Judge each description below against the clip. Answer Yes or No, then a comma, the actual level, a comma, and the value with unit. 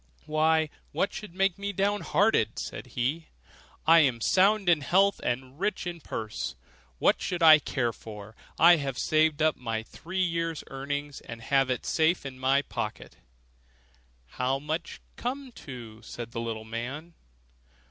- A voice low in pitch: No, medium, 150 Hz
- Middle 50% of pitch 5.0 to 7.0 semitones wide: Yes, wide, 5.5 semitones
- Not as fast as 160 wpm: No, average, 165 wpm